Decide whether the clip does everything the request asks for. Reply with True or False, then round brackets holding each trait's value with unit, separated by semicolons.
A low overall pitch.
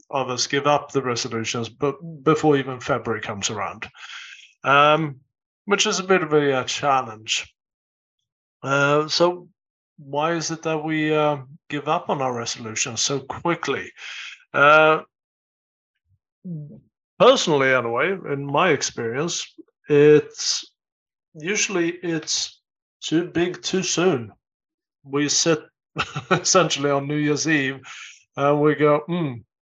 False (150 Hz)